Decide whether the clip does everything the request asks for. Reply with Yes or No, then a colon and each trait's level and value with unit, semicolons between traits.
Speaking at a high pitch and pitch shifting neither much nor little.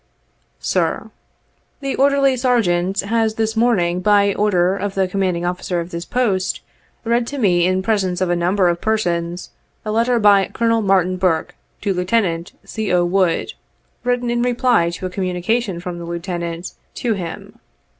Yes: high, 195 Hz; average, 4.2 semitones